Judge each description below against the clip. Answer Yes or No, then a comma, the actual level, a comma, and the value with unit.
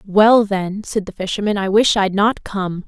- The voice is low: No, high, 200 Hz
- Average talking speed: No, fast, 210 wpm